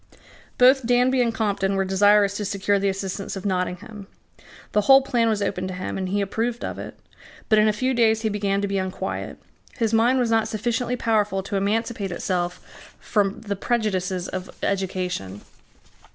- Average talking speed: Yes, average, 180 wpm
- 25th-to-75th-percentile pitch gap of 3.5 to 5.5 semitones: No, average, 2.8 semitones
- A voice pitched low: No, high, 205 Hz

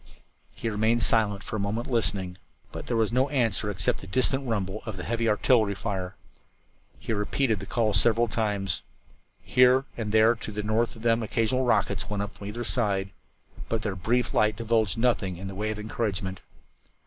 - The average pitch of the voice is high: No, low, 110 Hz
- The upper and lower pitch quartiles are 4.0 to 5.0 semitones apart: No, average, 2.7 semitones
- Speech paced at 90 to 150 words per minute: No, average, 185 wpm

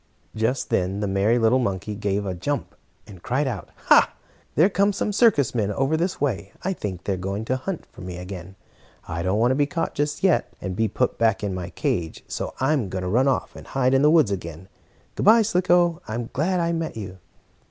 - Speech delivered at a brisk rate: Yes, fast, 225 wpm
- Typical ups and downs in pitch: No, wide, 7.8 semitones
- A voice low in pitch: Yes, low, 115 Hz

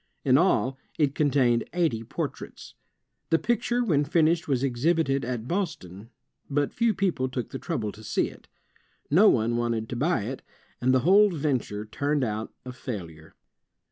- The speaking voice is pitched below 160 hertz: Yes, low, 135 Hz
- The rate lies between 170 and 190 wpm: No, average, 160 wpm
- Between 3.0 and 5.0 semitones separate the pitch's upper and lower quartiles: No, wide, 5.6 semitones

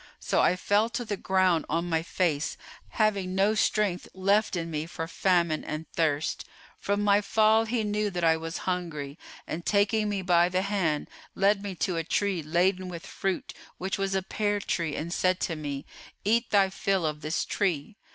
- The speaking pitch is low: No, medium, 185 Hz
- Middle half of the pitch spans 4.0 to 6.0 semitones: No, average, 3.6 semitones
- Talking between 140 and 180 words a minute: No, average, 190 wpm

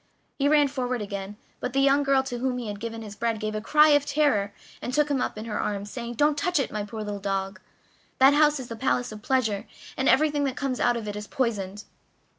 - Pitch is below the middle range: No, high, 245 Hz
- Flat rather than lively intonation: No, average, 4.7 semitones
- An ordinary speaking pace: No, fast, 250 wpm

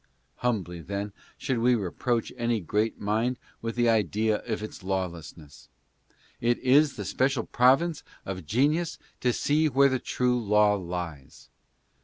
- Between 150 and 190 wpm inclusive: No, average, 140 wpm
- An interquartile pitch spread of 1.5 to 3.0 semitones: No, average, 4.6 semitones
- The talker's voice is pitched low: Yes, low, 115 Hz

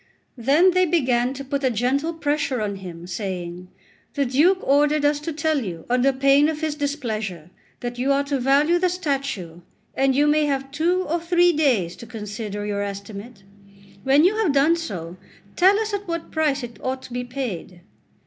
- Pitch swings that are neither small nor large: No, wide, 6.0 semitones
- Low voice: No, very high, 275 Hz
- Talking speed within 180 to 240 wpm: Yes, average, 185 wpm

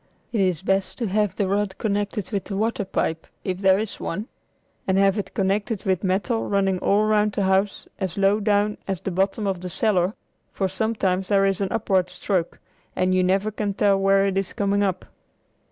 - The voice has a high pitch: Yes, high, 195 Hz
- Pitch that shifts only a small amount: Yes, narrow, 1.5 semitones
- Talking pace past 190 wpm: Yes, average, 200 wpm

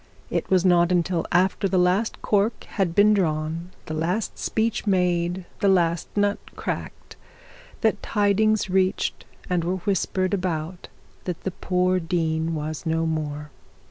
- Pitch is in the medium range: Yes, medium, 180 Hz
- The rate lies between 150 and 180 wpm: No, average, 140 wpm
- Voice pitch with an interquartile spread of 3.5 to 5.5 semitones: No, average, 2.9 semitones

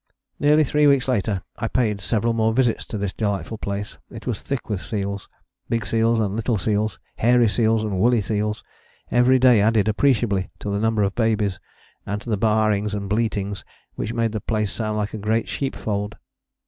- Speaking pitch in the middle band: No, low, 110 Hz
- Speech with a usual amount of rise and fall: No, narrow, 2.1 semitones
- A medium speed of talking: Yes, average, 185 wpm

